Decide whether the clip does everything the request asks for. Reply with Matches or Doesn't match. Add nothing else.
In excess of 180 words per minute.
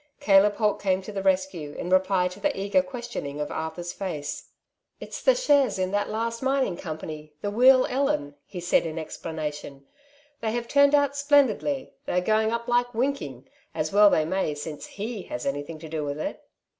Matches